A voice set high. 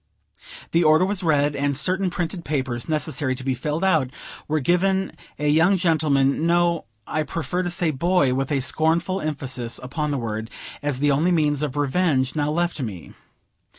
No: medium, 150 Hz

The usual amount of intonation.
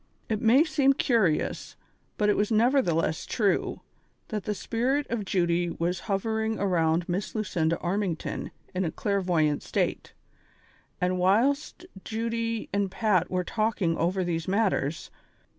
Yes: average, 4.3 semitones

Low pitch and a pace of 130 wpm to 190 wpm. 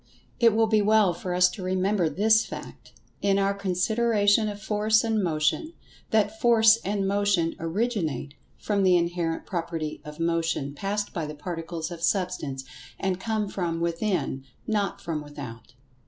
No: medium, 185 Hz; average, 155 wpm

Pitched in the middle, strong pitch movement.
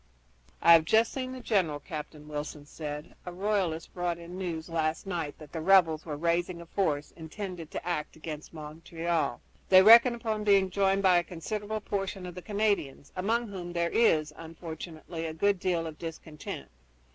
No: medium, 170 Hz; average, 3.6 semitones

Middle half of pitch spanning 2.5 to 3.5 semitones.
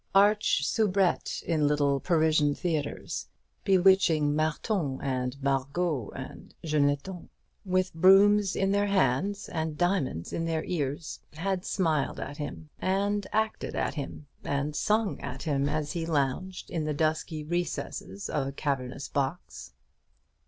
No: average, 4.7 semitones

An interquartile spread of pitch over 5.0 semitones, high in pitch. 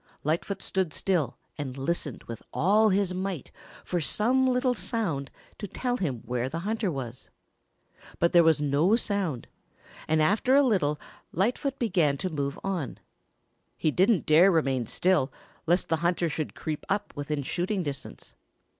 No: wide, 5.6 semitones; medium, 170 Hz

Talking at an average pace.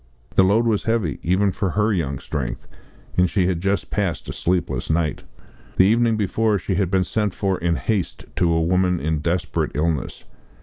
Yes: average, 185 wpm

